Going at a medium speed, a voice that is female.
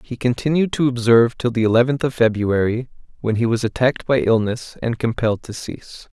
No: average, 185 wpm; male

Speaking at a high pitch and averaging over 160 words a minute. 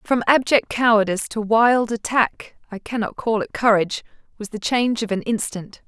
No: high, 220 Hz; average, 155 wpm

